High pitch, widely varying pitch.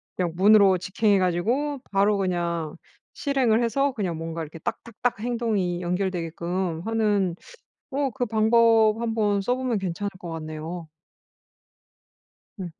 No: high, 200 Hz; average, 4.7 semitones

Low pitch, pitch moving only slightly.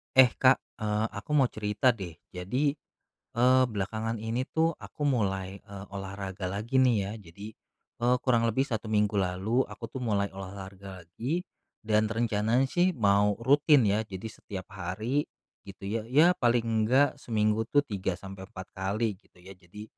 No: low, 110 Hz; average, 4.1 semitones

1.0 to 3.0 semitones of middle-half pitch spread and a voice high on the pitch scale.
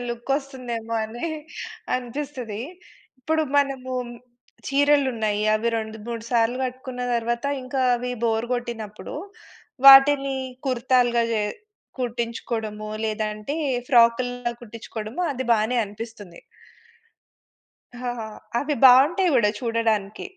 Yes: average, 2.7 semitones; high, 240 Hz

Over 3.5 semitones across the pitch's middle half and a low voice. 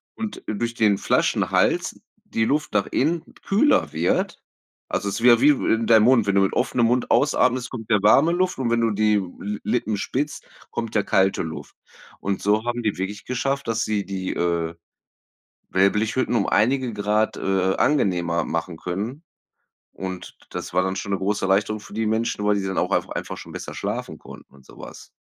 Yes: average, 3.9 semitones; low, 105 Hz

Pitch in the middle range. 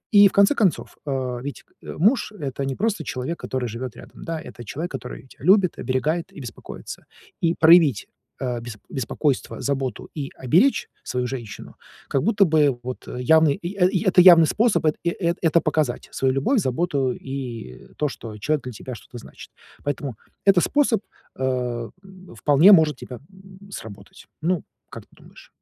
Yes: medium, 150 Hz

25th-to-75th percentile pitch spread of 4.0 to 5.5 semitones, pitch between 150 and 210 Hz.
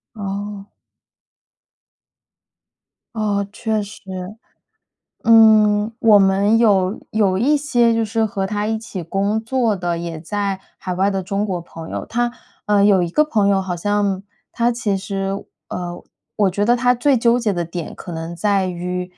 No: average, 2.8 semitones; high, 205 Hz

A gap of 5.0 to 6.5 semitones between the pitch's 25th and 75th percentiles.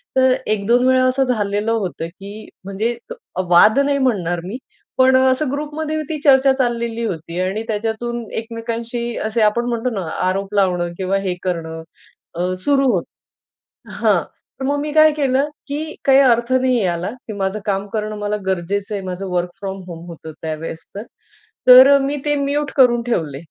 Yes: average, 5.3 semitones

